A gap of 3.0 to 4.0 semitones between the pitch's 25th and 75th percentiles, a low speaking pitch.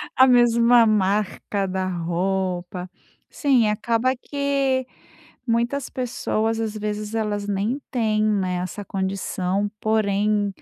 No: average, 3.3 semitones; high, 215 Hz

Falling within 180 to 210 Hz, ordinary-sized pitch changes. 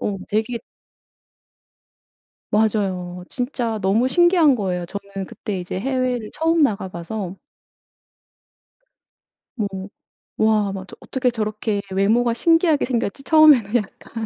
No: high, 220 Hz; average, 4.4 semitones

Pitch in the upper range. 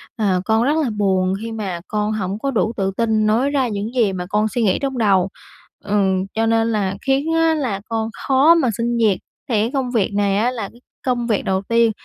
Yes: high, 220 Hz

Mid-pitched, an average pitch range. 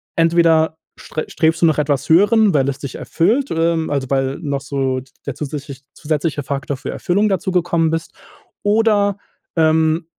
Yes: medium, 160 Hz; average, 3.5 semitones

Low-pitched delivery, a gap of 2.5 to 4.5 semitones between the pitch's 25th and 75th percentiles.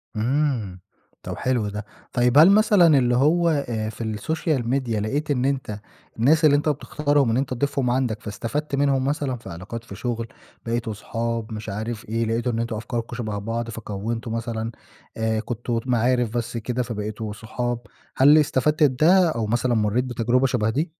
Yes: low, 120 Hz; average, 3.7 semitones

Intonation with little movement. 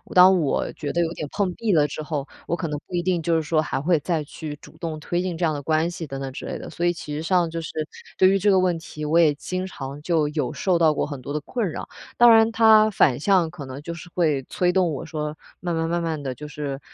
No: average, 3.1 semitones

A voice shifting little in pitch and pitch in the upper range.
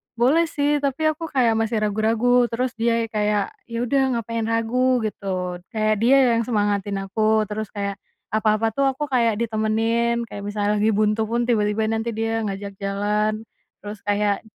Yes: narrow, 2.1 semitones; high, 220 Hz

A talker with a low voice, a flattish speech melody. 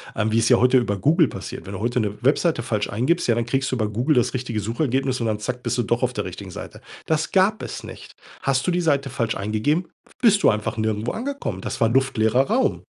No: low, 125 Hz; average, 5.0 semitones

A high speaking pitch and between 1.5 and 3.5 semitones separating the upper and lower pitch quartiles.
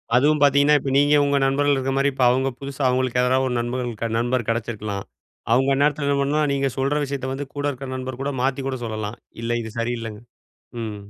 No: low, 130 Hz; average, 2.7 semitones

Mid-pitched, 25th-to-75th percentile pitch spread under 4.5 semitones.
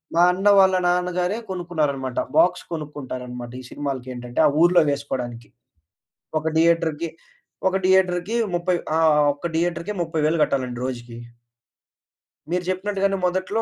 No: medium, 170 Hz; average, 5.3 semitones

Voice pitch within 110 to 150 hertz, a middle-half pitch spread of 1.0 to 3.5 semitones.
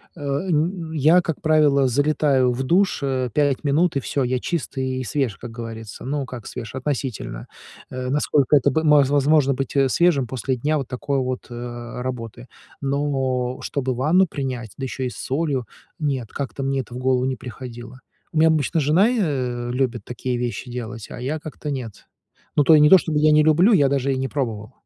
Yes: low, 135 Hz; average, 3.1 semitones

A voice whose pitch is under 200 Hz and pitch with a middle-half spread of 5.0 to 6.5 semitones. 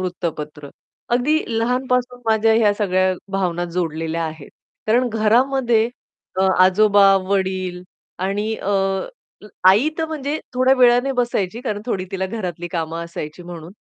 No: high, 205 Hz; wide, 5.4 semitones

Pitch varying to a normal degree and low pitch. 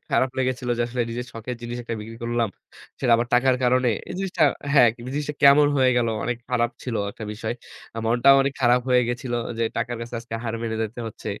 No: narrow, 1.7 semitones; low, 120 Hz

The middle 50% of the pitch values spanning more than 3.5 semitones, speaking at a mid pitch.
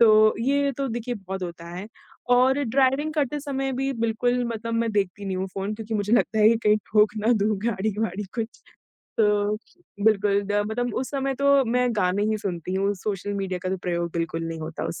No: average, 3.9 semitones; high, 215 Hz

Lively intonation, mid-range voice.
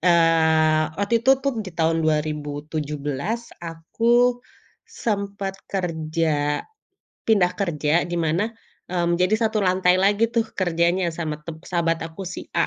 No: average, 4.0 semitones; medium, 170 Hz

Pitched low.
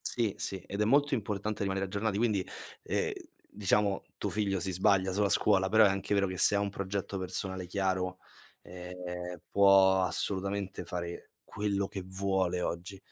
Yes: very low, 95 Hz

